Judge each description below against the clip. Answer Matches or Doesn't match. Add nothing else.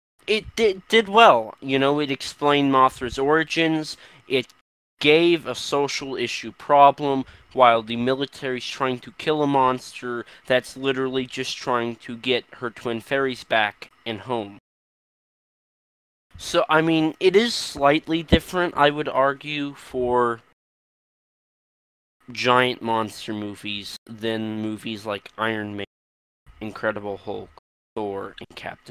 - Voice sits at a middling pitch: Doesn't match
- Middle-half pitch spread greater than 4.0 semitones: Matches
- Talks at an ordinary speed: Doesn't match